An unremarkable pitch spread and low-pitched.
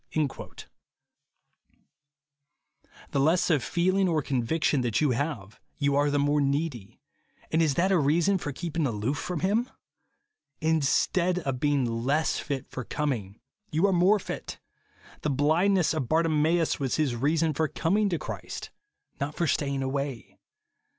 No: average, 3.6 semitones; medium, 150 Hz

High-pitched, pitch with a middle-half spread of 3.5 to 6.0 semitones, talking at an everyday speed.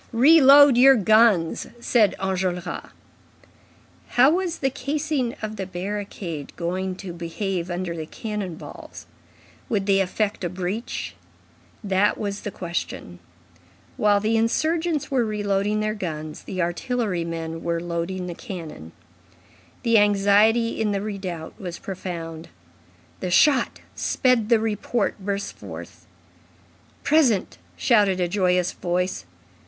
No: high, 200 Hz; average, 4.3 semitones; slow, 125 wpm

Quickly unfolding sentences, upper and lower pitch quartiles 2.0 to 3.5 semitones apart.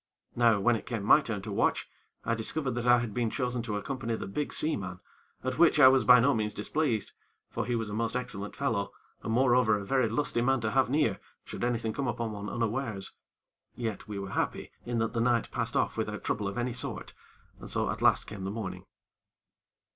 Yes: fast, 220 wpm; average, 2.8 semitones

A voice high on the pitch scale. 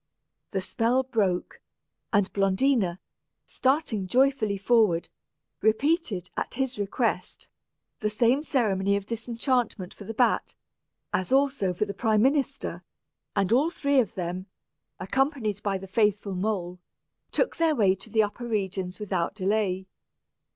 Yes: high, 210 Hz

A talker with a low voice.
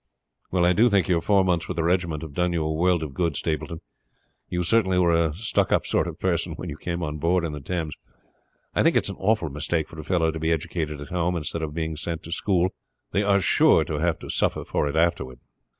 Yes: very low, 85 Hz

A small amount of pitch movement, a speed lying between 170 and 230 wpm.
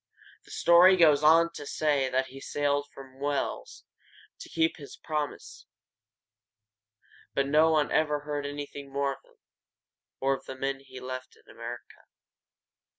No: narrow, 1.9 semitones; average, 150 wpm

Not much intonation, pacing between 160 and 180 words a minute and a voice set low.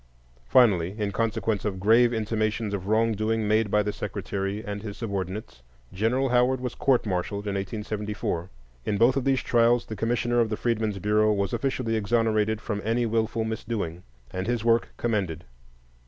Yes: narrow, 2.3 semitones; average, 170 wpm; low, 110 Hz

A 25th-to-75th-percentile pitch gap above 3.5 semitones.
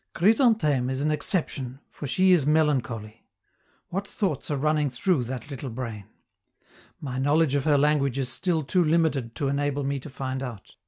No: average, 3.1 semitones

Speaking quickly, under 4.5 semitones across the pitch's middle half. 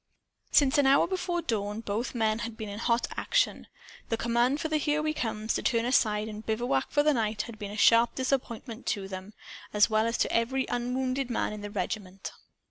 Yes: fast, 210 wpm; average, 3.5 semitones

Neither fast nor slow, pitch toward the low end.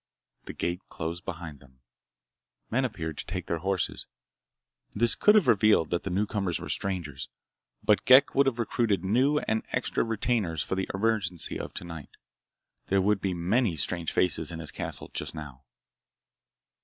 Yes: average, 160 wpm; very low, 95 Hz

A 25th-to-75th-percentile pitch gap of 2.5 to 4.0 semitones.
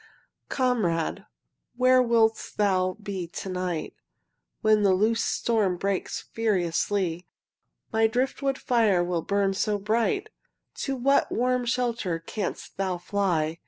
No: average, 4.4 semitones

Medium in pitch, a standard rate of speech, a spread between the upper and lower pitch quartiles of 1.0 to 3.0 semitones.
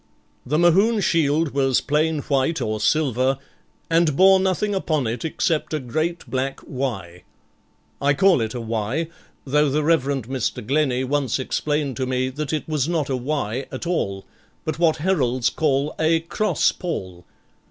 No: medium, 145 Hz; average, 160 wpm; average, 3.8 semitones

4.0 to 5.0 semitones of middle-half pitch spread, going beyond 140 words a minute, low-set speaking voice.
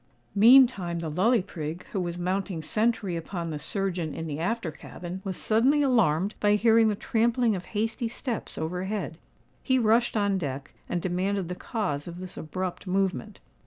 No: average, 4.4 semitones; average, 170 wpm; high, 190 Hz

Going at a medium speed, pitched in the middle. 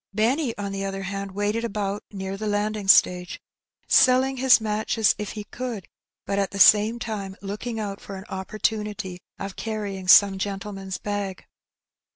No: average, 160 wpm; high, 205 Hz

